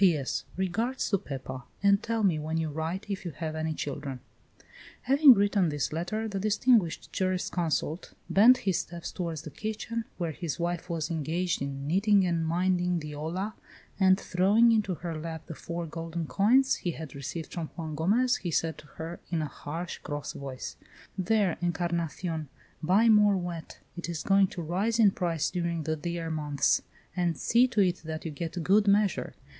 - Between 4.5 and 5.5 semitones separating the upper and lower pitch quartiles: No, average, 3.8 semitones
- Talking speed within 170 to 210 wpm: Yes, average, 180 wpm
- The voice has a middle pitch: Yes, medium, 175 Hz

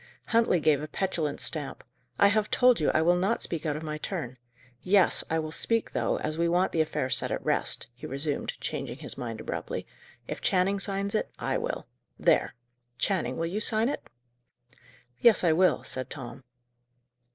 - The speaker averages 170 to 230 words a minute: Yes, average, 185 wpm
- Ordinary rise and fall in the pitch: Yes, average, 4.6 semitones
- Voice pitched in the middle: Yes, medium, 170 Hz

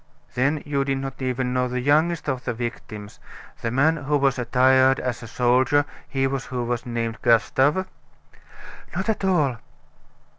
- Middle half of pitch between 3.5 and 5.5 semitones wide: No, narrow, 2.4 semitones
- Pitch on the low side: Yes, low, 130 Hz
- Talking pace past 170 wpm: No, average, 155 wpm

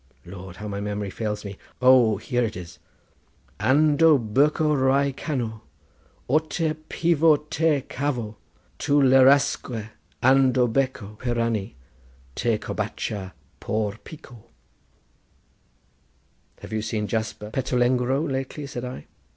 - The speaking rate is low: Yes, slow, 110 wpm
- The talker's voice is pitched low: Yes, low, 125 Hz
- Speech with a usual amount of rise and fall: Yes, average, 4.5 semitones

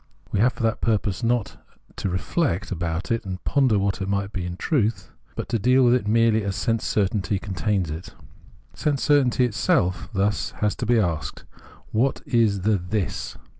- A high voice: No, low, 105 Hz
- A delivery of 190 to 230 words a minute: Yes, average, 195 wpm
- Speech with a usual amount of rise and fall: Yes, average, 3.5 semitones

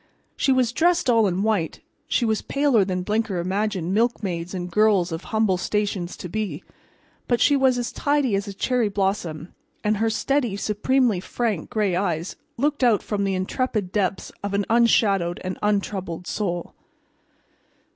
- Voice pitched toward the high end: Yes, high, 205 Hz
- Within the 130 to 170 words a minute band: Yes, average, 160 wpm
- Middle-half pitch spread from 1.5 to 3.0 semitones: No, average, 4.0 semitones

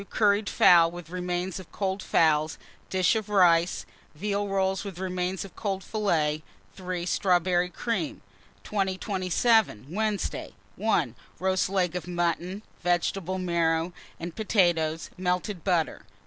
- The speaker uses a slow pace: Yes, slow, 120 wpm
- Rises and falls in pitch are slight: Yes, narrow, 2.3 semitones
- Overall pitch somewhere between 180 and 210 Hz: Yes, medium, 185 Hz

